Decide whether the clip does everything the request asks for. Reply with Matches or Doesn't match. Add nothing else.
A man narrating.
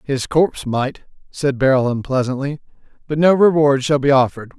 Matches